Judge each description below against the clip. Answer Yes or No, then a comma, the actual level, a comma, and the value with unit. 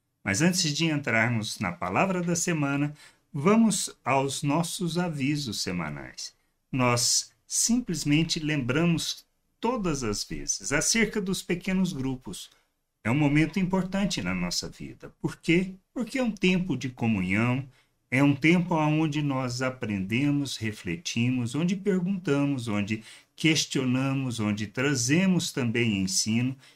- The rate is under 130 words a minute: Yes, slow, 120 wpm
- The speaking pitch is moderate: Yes, medium, 145 Hz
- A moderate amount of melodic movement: No, wide, 6.3 semitones